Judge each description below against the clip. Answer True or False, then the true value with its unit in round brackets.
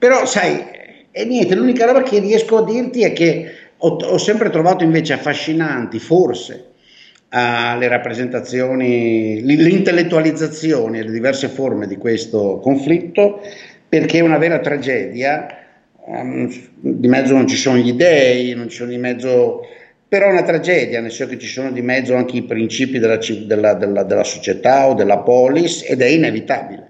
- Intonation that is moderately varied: False (5.7 semitones)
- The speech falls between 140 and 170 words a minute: True (150 wpm)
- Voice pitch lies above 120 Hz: True (135 Hz)